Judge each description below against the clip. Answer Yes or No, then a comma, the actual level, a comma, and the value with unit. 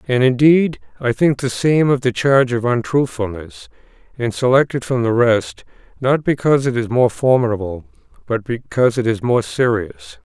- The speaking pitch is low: Yes, low, 125 Hz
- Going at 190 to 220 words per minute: No, average, 170 wpm